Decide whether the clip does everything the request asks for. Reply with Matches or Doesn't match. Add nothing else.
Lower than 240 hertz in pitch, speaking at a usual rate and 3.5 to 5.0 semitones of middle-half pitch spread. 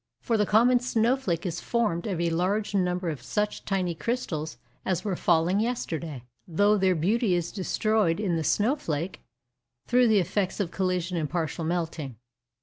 Matches